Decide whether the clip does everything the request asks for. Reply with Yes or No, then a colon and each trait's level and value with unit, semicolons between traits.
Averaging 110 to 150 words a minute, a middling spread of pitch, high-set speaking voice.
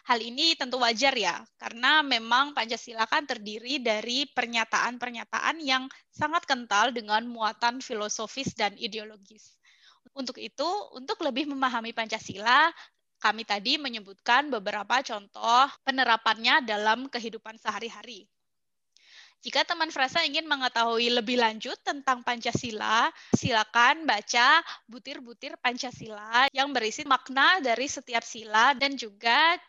Yes: average, 115 wpm; average, 3.7 semitones; high, 245 Hz